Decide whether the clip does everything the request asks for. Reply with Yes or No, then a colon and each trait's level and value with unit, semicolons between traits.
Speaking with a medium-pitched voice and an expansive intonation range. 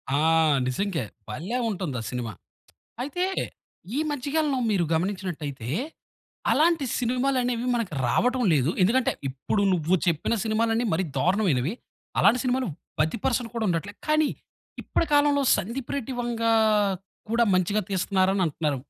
No: high, 215 Hz; wide, 6.6 semitones